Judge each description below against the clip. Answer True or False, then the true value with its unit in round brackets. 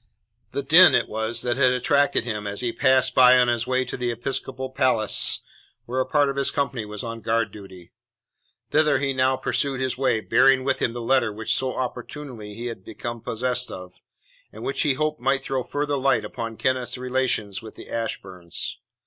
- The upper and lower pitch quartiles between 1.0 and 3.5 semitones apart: True (2.8 semitones)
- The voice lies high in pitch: False (125 Hz)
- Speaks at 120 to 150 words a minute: False (195 wpm)